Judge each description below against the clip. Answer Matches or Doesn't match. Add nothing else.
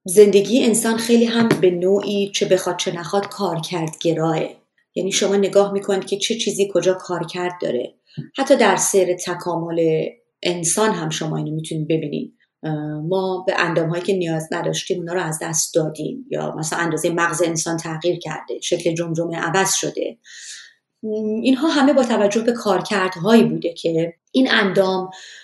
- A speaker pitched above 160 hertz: Matches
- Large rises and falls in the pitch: Doesn't match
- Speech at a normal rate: Doesn't match